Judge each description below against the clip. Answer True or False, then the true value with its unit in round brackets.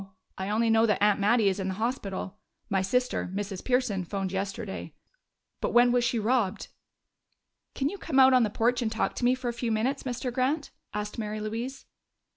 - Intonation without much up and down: False (3.6 semitones)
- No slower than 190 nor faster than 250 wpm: True (200 wpm)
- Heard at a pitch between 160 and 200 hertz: False (225 Hz)